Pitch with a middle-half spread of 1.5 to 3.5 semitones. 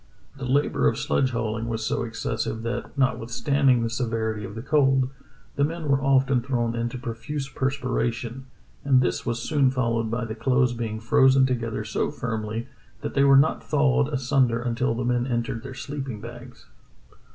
Yes: narrow, 2.6 semitones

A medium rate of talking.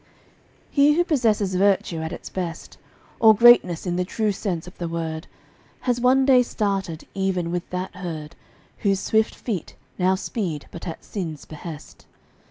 Yes: average, 160 wpm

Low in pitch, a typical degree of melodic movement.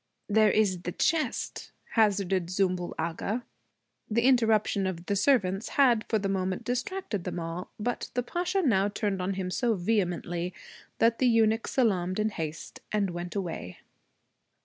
No: high, 200 Hz; average, 3.9 semitones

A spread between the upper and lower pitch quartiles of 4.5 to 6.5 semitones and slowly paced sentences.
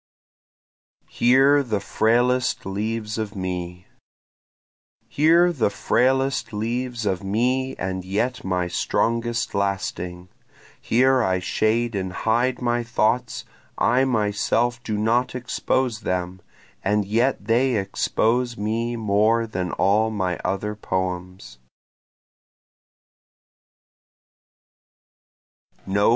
No: average, 4.0 semitones; slow, 95 wpm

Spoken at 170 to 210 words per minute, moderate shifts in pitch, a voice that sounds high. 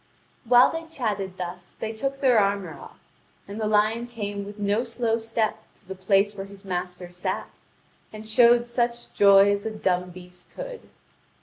Yes: average, 180 wpm; average, 3.3 semitones; high, 210 Hz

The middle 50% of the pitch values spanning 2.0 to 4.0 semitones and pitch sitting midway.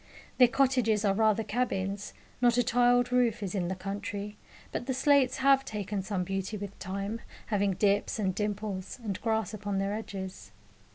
No: average, 3.3 semitones; high, 210 Hz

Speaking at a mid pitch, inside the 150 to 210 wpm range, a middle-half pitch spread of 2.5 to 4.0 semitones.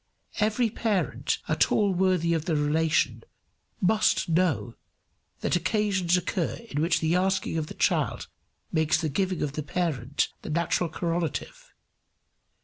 No: medium, 170 Hz; average, 140 wpm; average, 3.2 semitones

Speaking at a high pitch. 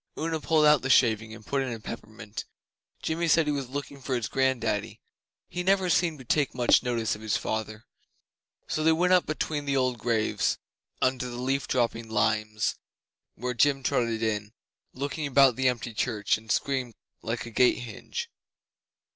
No: low, 125 Hz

